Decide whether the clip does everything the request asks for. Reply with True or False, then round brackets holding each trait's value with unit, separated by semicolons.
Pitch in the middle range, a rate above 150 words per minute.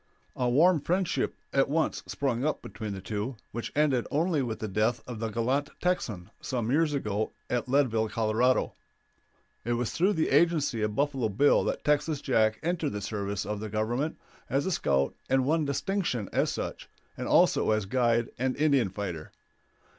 False (125 Hz; 175 wpm)